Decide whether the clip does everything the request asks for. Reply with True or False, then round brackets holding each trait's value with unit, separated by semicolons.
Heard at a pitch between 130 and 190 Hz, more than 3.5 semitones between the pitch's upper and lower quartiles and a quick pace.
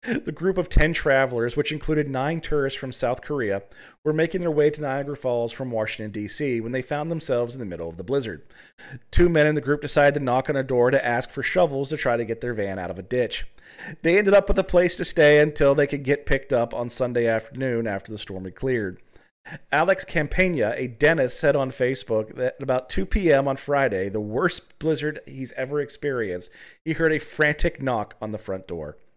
True (135 Hz; 4.2 semitones; 220 wpm)